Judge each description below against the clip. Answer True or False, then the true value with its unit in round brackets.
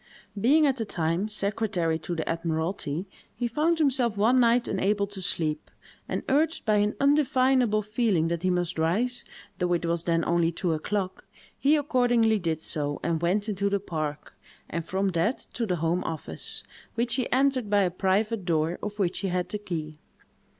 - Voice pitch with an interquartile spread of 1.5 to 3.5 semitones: False (5.6 semitones)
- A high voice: True (200 Hz)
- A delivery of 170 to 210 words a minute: True (180 wpm)